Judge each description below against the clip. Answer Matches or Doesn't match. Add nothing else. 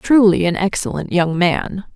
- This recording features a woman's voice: Matches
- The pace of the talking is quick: Doesn't match